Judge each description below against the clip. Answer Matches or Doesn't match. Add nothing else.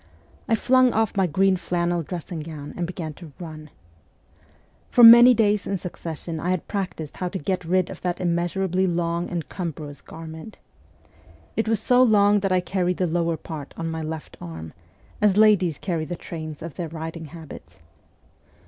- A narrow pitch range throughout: Doesn't match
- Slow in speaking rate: Doesn't match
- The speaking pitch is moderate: Matches